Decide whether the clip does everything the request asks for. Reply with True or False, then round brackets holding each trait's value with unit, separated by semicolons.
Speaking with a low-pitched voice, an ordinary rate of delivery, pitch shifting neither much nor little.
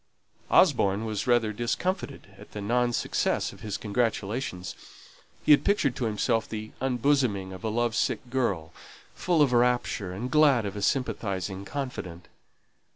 True (115 Hz; 150 wpm; 4.0 semitones)